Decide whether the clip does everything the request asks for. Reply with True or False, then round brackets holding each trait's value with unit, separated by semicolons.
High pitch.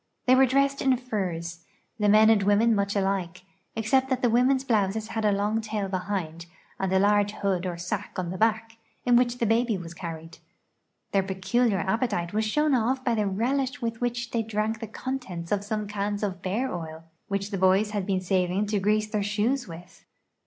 True (210 Hz)